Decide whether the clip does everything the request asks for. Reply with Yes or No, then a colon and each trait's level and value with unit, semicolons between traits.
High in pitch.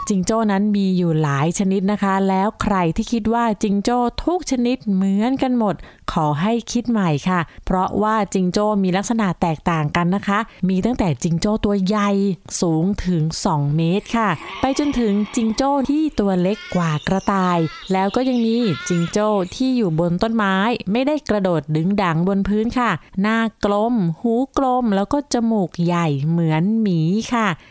Yes: high, 200 Hz